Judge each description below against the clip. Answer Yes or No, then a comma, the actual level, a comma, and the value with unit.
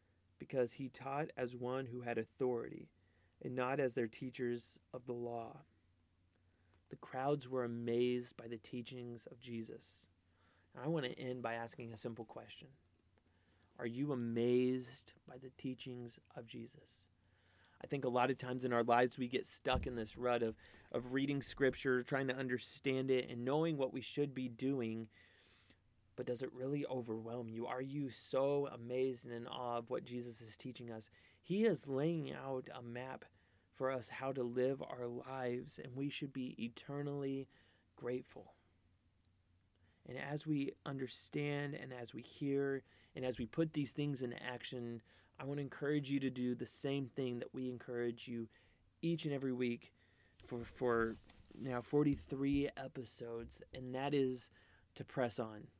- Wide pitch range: No, average, 2.9 semitones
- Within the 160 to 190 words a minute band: Yes, average, 170 wpm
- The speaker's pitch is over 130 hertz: No, low, 125 Hz